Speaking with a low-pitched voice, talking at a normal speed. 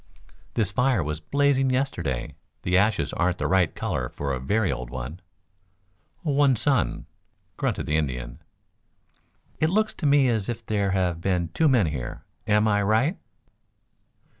Yes: low, 100 Hz; average, 150 wpm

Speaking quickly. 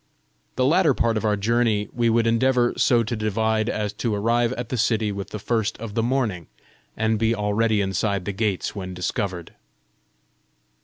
No: average, 175 wpm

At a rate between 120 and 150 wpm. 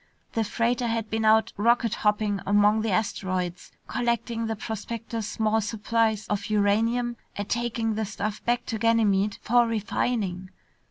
Yes: average, 145 wpm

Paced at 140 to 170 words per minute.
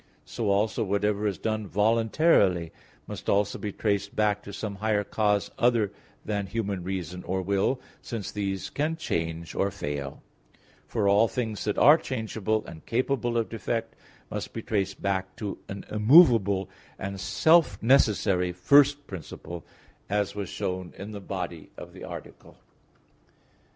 Yes: average, 145 wpm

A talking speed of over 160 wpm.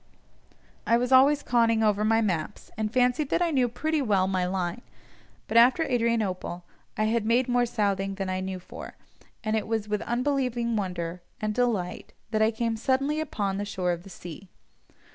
Yes: average, 180 wpm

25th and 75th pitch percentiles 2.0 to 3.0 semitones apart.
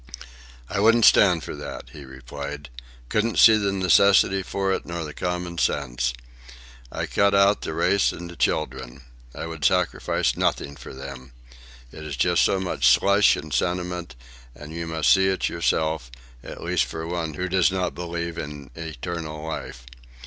No: average, 4.2 semitones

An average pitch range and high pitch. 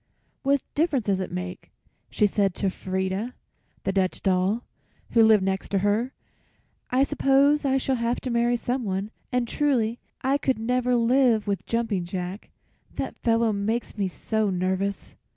Yes: average, 4.4 semitones; high, 220 Hz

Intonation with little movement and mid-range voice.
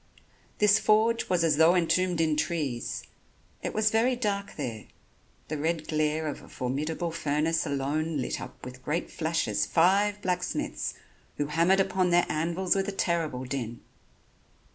No: average, 3.9 semitones; medium, 165 Hz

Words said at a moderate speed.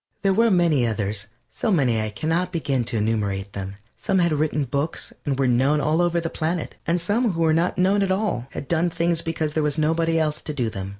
No: fast, 235 wpm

